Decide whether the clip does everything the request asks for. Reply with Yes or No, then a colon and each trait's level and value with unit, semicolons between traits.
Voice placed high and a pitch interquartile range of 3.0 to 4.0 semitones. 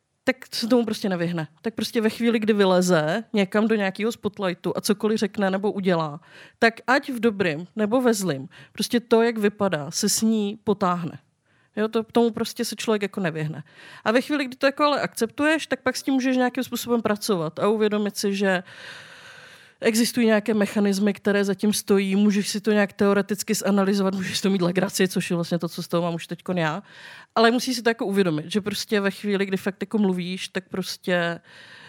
Yes: high, 205 Hz; average, 3.7 semitones